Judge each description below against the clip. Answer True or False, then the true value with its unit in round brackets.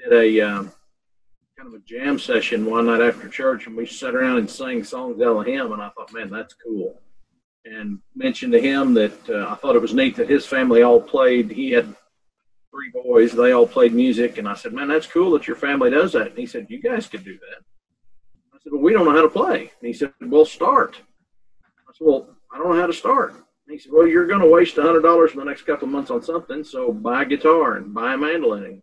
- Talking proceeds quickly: True (250 wpm)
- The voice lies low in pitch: False (175 Hz)